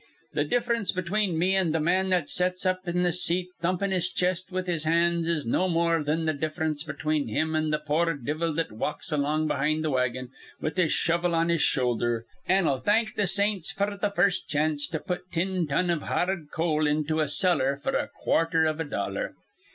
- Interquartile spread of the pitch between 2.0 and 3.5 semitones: Yes, average, 3.2 semitones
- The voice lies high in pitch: No, medium, 165 Hz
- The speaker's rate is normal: No, fast, 210 wpm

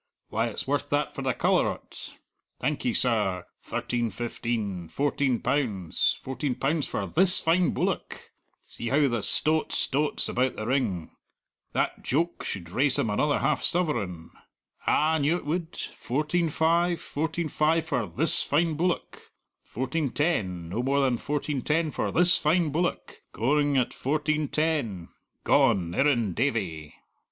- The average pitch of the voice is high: No, medium, 140 Hz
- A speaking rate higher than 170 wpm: No, average, 145 wpm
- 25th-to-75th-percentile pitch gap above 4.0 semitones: Yes, average, 5.2 semitones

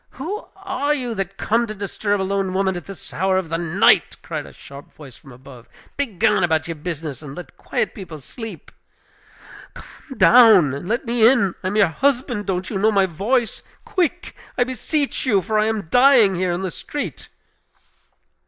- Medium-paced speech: Yes, average, 190 wpm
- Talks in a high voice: Yes, high, 200 Hz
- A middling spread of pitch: No, wide, 5.7 semitones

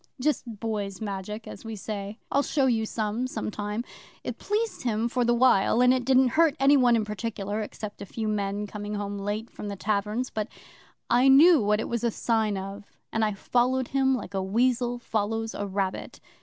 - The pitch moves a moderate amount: Yes, average, 3.3 semitones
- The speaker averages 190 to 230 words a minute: Yes, average, 200 wpm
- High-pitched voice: Yes, high, 220 Hz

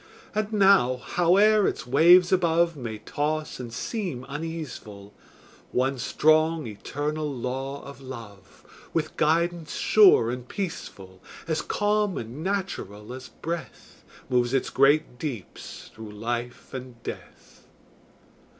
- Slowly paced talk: Yes, slow, 115 wpm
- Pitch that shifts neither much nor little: No, wide, 5.8 semitones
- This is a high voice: No, medium, 140 Hz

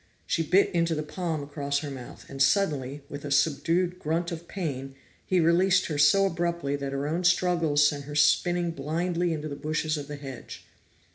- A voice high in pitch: No, medium, 155 Hz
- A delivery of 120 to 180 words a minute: No, average, 190 wpm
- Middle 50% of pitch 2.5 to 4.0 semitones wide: Yes, average, 3.3 semitones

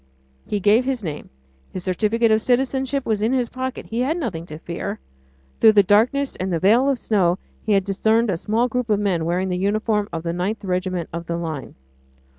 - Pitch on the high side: Yes, high, 210 Hz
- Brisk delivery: Yes, fast, 210 wpm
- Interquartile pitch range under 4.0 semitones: No, average, 4.7 semitones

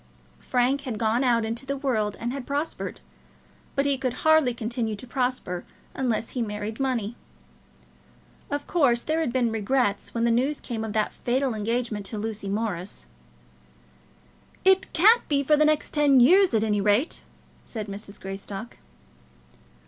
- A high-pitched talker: Yes, high, 240 Hz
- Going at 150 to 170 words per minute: Yes, average, 155 wpm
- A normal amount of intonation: Yes, average, 4.3 semitones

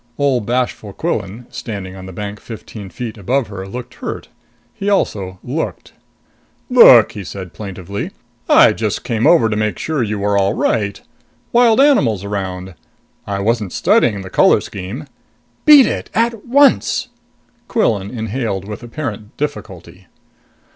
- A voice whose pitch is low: Yes, low, 105 Hz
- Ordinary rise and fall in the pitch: Yes, average, 4.8 semitones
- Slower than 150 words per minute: Yes, average, 140 wpm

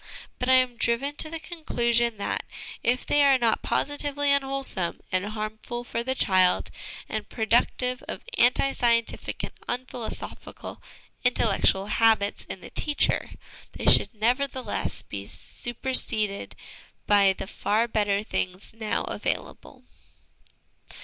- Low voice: No, high, 235 Hz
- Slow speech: Yes, slow, 125 wpm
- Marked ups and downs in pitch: No, average, 3.6 semitones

